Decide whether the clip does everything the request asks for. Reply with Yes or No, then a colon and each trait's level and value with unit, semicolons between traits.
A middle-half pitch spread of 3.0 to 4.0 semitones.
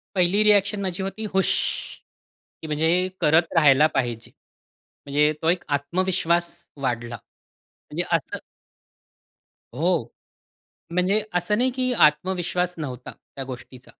No: average, 4.8 semitones